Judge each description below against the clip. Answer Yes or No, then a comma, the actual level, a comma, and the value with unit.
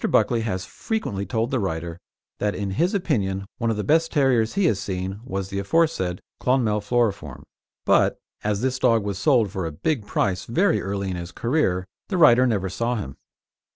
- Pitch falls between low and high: No, low, 105 Hz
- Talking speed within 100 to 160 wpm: No, average, 190 wpm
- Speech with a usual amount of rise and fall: Yes, average, 5.0 semitones